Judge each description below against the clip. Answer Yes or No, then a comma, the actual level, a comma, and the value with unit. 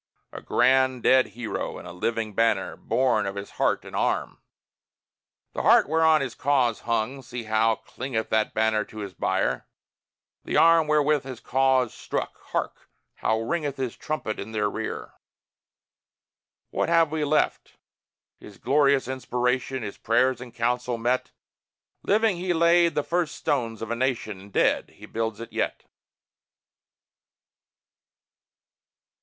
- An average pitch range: Yes, average, 4.3 semitones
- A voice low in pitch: Yes, low, 125 Hz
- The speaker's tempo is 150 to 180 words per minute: No, average, 140 wpm